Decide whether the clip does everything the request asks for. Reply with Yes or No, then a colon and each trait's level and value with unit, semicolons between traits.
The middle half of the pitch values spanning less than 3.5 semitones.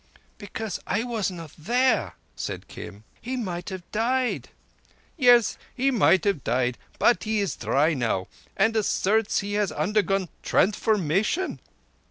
No: average, 4.7 semitones